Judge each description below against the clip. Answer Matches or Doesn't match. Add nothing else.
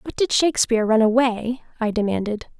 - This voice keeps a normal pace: Matches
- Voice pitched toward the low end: Doesn't match